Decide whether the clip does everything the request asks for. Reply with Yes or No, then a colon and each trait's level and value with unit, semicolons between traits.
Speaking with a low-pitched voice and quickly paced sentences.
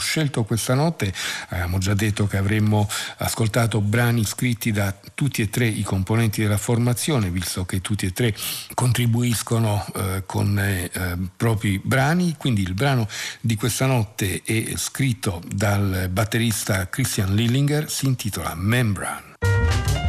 No: low, 110 Hz; average, 135 wpm